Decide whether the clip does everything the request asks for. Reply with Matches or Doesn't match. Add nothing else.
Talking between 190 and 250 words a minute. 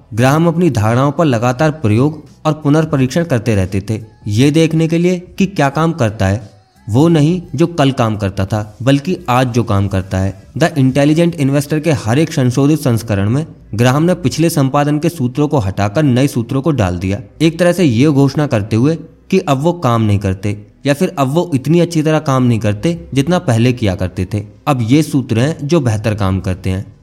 Matches